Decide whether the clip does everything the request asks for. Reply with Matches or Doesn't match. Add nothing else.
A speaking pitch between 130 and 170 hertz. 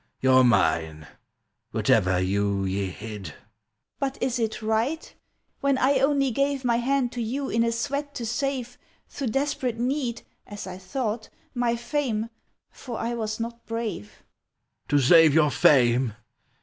Doesn't match